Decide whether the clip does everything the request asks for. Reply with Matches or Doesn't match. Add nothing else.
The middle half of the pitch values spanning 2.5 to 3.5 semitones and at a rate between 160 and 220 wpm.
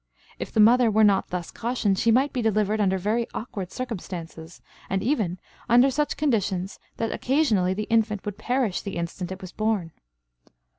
Doesn't match